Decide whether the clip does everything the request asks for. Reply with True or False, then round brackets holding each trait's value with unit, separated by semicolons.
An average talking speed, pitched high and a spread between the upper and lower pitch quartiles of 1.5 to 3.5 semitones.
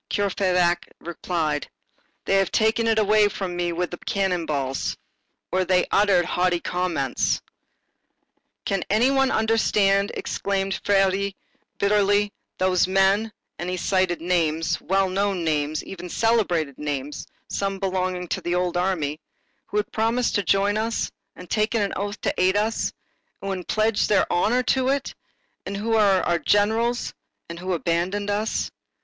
True (145 wpm; 195 Hz; 2.8 semitones)